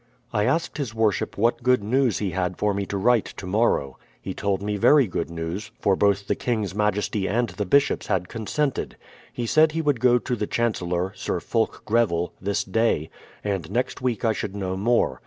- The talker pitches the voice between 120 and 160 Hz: No, low, 105 Hz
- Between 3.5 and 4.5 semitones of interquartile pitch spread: Yes, average, 3.8 semitones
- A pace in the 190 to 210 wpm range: Yes, fast, 205 wpm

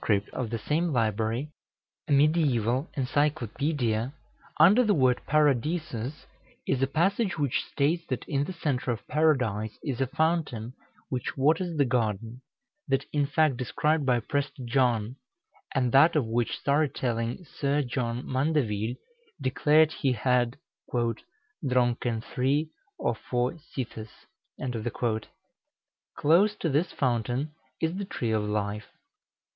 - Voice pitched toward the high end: No, low, 135 Hz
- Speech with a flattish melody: No, average, 4.2 semitones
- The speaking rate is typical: No, slow, 125 wpm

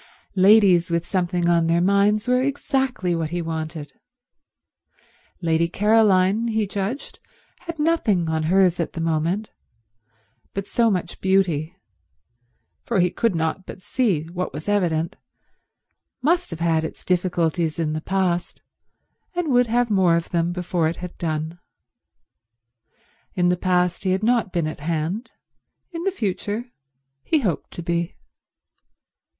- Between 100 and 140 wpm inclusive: Yes, slow, 135 wpm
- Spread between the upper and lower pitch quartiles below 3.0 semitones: No, average, 4.0 semitones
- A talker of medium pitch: Yes, medium, 180 Hz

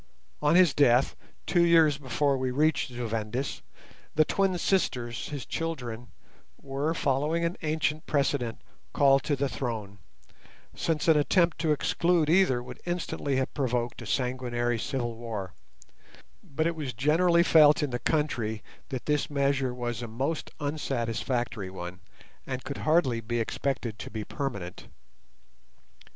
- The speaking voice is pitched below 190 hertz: Yes, low, 135 Hz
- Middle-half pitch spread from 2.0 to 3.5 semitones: No, average, 4.3 semitones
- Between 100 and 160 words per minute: Yes, average, 140 wpm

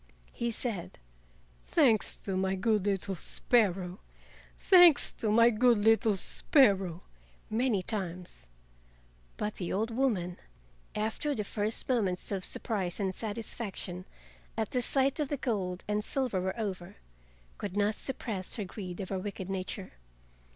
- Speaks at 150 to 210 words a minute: No, slow, 135 wpm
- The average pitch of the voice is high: Yes, high, 210 Hz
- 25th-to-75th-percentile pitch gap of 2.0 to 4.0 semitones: Yes, average, 3.7 semitones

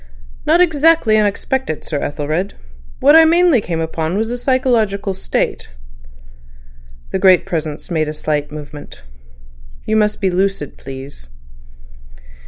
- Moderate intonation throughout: No, wide, 8.1 semitones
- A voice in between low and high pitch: No, high, 195 Hz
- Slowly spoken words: Yes, slow, 125 wpm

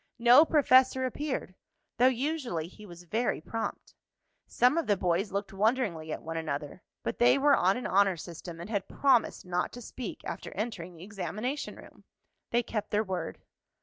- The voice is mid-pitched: No, high, 210 Hz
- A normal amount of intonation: No, wide, 6.0 semitones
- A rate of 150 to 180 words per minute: Yes, average, 175 wpm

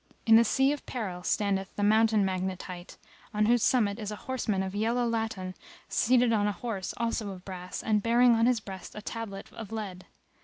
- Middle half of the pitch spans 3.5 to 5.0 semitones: No, average, 3.1 semitones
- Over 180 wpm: Yes, average, 200 wpm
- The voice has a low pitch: No, high, 210 Hz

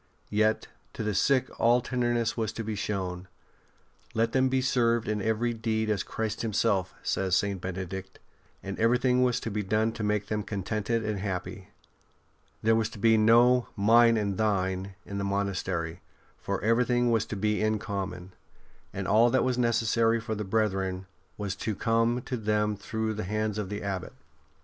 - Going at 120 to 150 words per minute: No, average, 185 wpm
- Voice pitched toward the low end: Yes, low, 110 Hz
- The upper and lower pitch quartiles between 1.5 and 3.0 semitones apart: Yes, narrow, 2.6 semitones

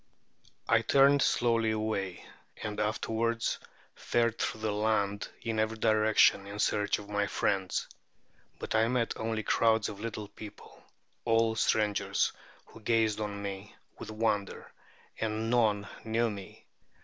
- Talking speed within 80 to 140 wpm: Yes, slow, 135 wpm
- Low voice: Yes, low, 110 Hz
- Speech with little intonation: Yes, narrow, 1.6 semitones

